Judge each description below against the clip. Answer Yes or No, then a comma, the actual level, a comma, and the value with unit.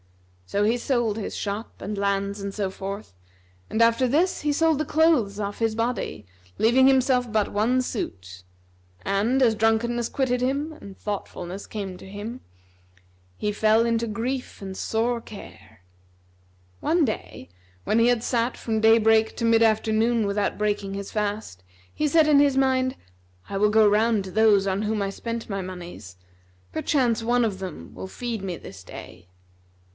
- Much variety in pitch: No, average, 3.4 semitones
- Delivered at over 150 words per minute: Yes, average, 170 wpm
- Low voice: No, high, 220 Hz